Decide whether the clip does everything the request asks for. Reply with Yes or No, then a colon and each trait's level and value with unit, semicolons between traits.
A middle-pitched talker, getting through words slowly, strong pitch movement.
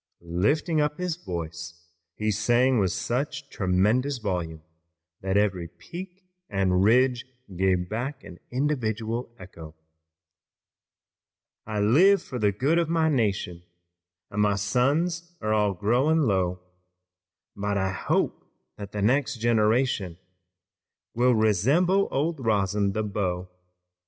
No: low, 110 Hz; slow, 120 wpm; wide, 6.2 semitones